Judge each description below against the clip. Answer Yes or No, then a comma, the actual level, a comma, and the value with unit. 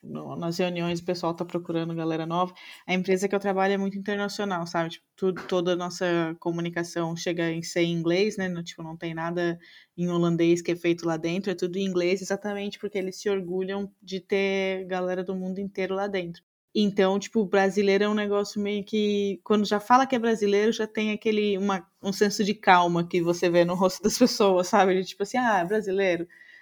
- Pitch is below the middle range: No, high, 190 Hz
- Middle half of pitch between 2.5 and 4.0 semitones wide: Yes, average, 2.8 semitones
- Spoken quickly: Yes, fast, 210 wpm